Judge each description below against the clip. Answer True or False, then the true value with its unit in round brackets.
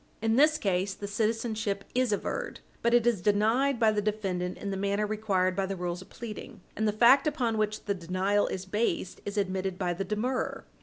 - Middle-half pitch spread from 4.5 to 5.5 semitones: False (2.8 semitones)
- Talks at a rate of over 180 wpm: True (205 wpm)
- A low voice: False (210 Hz)